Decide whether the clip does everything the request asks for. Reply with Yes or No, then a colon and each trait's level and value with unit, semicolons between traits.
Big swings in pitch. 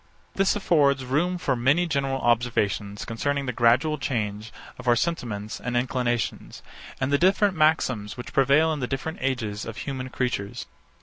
No: average, 3.9 semitones